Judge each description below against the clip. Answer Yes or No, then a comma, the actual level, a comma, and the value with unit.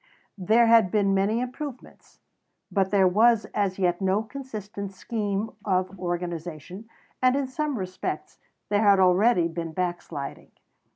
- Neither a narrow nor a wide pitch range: Yes, average, 3.7 semitones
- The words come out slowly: Yes, slow, 130 wpm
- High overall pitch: Yes, high, 195 Hz